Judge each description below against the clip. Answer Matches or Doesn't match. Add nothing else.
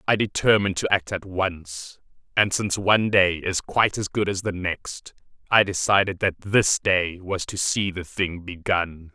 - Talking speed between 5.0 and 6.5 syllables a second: Doesn't match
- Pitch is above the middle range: Doesn't match